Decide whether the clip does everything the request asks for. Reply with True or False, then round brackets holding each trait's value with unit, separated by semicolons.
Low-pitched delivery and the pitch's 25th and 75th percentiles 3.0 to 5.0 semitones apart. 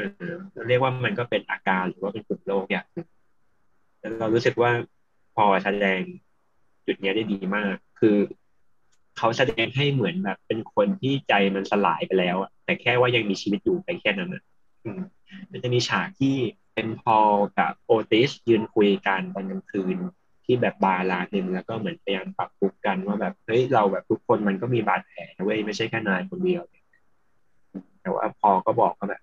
False (110 Hz; 5.5 semitones)